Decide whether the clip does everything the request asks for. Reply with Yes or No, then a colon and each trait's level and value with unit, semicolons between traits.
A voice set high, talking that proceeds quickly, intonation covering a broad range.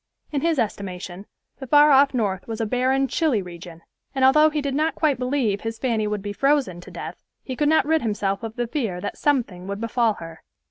Yes: high, 235 Hz; fast, 220 wpm; wide, 5.7 semitones